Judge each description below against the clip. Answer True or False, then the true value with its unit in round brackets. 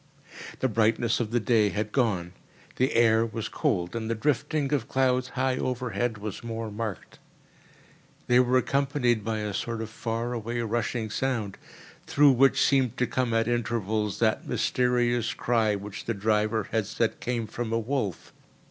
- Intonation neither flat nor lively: False (2.3 semitones)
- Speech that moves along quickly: False (165 wpm)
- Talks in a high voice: False (115 Hz)